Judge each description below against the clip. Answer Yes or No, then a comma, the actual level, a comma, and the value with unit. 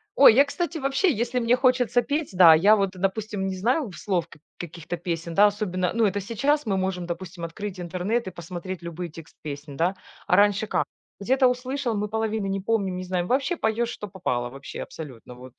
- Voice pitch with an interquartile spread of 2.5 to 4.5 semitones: No, average, 5.1 semitones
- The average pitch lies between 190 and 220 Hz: Yes, high, 195 Hz